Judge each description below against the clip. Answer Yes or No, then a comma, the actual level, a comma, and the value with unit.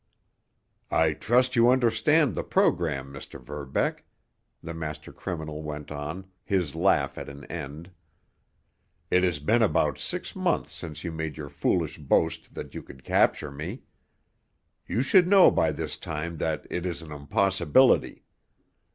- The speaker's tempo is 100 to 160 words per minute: Yes, average, 145 wpm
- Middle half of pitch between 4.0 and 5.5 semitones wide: Yes, average, 4.5 semitones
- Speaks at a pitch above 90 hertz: No, very low, 80 Hz